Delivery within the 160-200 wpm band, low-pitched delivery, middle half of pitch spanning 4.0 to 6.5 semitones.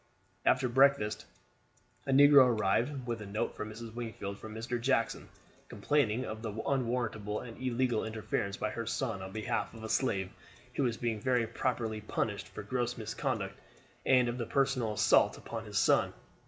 No: average, 170 wpm; low, 115 Hz; average, 2.8 semitones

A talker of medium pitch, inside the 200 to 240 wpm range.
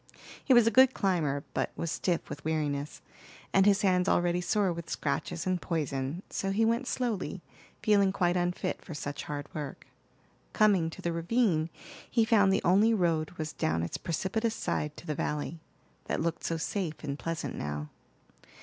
No: medium, 175 Hz; average, 175 wpm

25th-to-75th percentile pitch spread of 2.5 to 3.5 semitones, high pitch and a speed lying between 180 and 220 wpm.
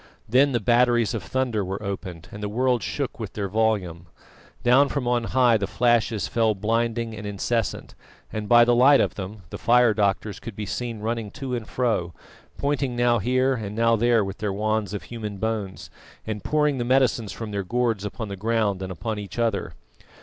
No: average, 2.8 semitones; low, 110 Hz; average, 195 wpm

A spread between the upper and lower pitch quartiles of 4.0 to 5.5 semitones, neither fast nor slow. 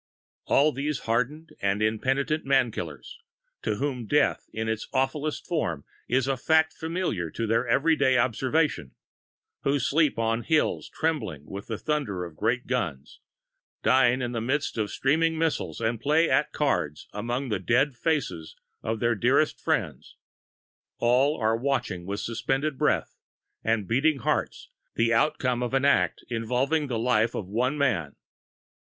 Yes: average, 4.4 semitones; average, 150 wpm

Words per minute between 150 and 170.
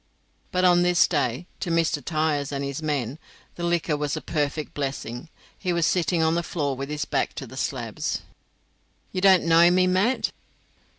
No: average, 180 wpm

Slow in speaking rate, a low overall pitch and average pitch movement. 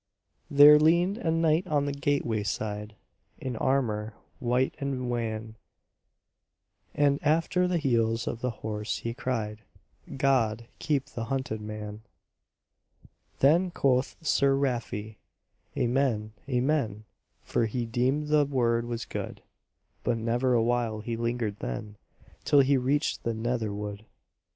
Yes: slow, 130 wpm; low, 120 Hz; average, 4.1 semitones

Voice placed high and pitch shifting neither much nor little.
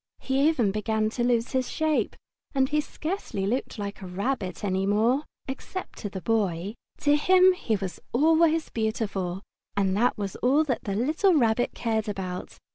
No: high, 225 Hz; wide, 6.3 semitones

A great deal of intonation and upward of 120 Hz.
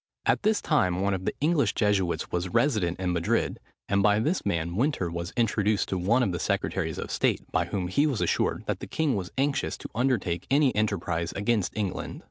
No: wide, 6.2 semitones; low, 100 Hz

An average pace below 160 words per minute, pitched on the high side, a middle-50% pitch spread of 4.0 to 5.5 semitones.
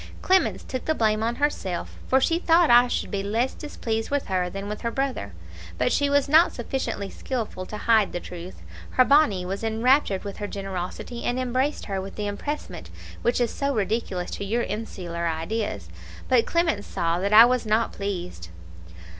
No: average, 185 wpm; high, 225 Hz; average, 4.9 semitones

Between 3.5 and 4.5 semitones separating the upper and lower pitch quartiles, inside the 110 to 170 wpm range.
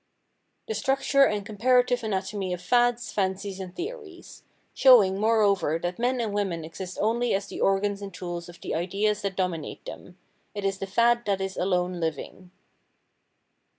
Yes: average, 4.1 semitones; average, 160 wpm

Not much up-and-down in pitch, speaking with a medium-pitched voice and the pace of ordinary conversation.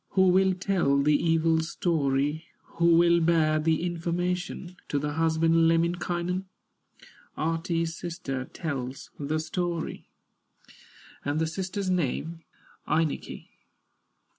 No: narrow, 2.0 semitones; medium, 165 Hz; slow, 105 wpm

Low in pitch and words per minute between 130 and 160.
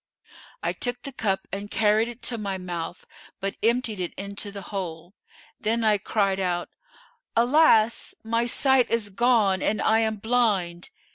No: high, 215 Hz; average, 155 wpm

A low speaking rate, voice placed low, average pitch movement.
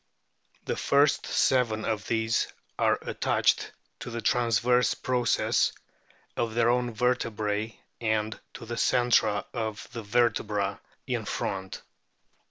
No: slow, 115 wpm; low, 115 Hz; narrow, 2.2 semitones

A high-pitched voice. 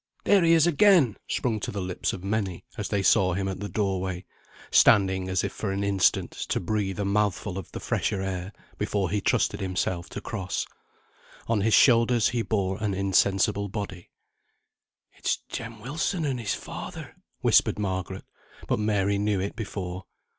No: low, 100 Hz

